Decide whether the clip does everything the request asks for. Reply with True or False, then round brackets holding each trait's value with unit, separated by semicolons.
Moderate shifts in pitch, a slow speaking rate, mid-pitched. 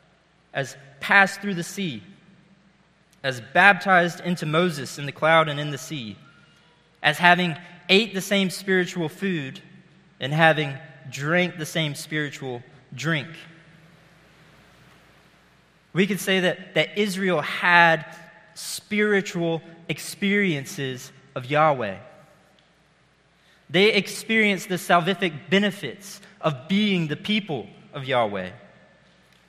True (3.7 semitones; 105 wpm; 170 Hz)